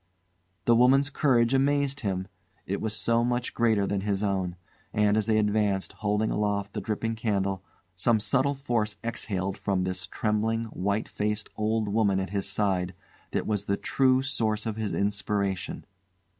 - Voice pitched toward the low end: Yes, low, 105 Hz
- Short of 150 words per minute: No, average, 160 wpm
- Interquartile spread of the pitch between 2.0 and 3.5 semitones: Yes, narrow, 2.6 semitones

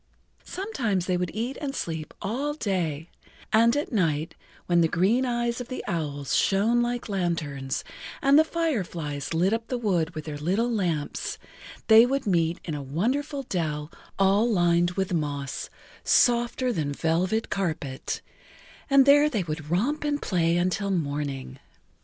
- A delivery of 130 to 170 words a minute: Yes, average, 150 wpm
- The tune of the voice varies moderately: No, wide, 6.9 semitones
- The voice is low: No, medium, 185 Hz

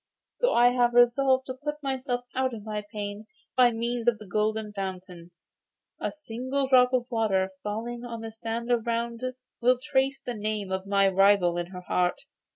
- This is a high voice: Yes, high, 230 Hz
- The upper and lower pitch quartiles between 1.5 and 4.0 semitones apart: Yes, average, 3.6 semitones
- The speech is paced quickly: No, average, 180 wpm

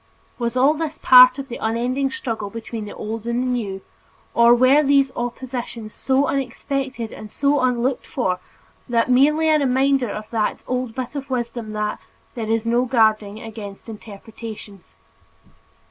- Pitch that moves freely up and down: No, average, 3.1 semitones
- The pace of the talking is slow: No, average, 150 wpm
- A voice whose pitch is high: Yes, high, 240 Hz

